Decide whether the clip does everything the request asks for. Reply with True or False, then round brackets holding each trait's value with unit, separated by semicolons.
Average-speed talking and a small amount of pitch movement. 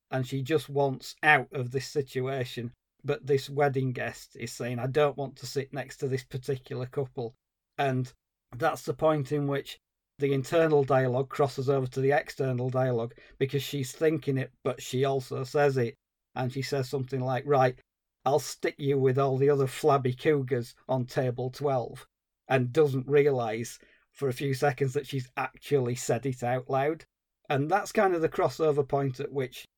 True (180 wpm; 1.9 semitones)